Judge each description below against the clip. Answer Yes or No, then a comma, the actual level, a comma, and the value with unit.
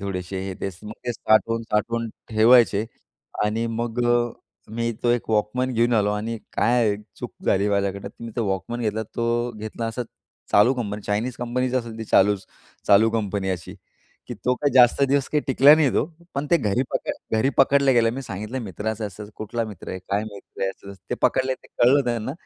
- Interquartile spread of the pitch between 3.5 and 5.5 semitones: No, average, 2.9 semitones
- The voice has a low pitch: Yes, low, 115 Hz